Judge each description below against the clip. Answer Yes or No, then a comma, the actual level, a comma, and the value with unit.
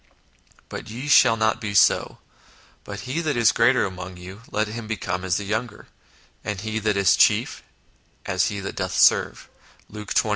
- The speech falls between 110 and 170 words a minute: No, average, 185 wpm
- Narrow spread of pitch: Yes, narrow, 2.3 semitones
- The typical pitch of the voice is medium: No, low, 105 Hz